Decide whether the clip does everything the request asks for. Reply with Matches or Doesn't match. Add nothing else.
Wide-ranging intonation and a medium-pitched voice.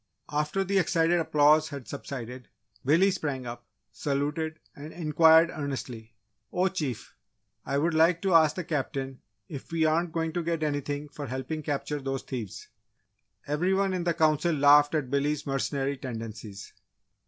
Doesn't match